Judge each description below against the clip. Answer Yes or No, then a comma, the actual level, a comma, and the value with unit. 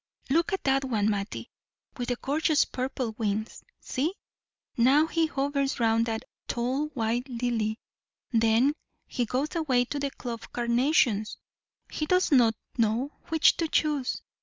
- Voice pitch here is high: Yes, very high, 255 Hz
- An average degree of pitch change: Yes, average, 4.1 semitones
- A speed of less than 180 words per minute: Yes, average, 140 wpm